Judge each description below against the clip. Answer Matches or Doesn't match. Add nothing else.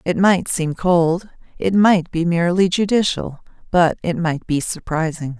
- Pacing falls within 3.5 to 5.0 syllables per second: Matches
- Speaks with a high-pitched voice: Doesn't match